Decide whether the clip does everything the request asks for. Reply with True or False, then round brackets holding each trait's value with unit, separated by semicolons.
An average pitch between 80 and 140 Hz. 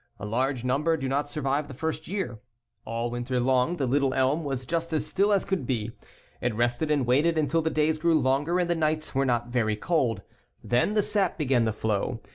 True (135 Hz)